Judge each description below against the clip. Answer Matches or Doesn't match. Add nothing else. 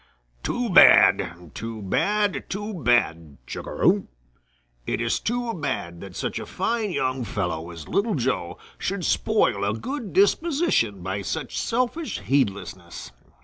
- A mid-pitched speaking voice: Doesn't match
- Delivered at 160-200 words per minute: Doesn't match